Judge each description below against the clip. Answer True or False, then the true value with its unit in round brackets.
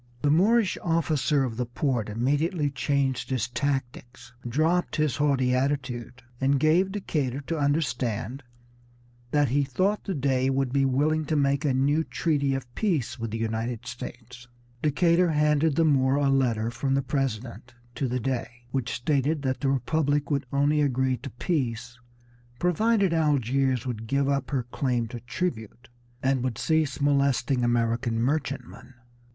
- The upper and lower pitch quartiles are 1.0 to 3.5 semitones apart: True (3.2 semitones)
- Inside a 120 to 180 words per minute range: True (155 wpm)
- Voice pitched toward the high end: False (135 Hz)